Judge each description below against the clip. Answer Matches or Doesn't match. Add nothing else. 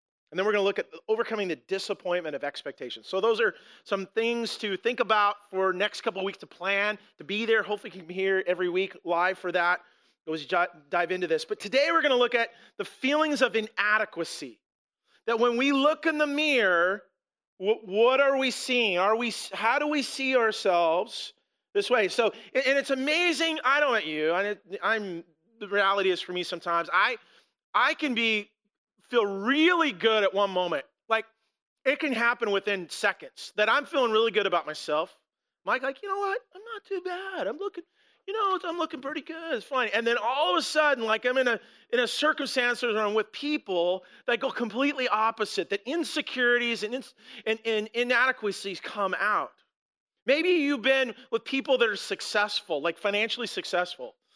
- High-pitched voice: Matches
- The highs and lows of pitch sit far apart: Matches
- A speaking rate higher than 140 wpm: Matches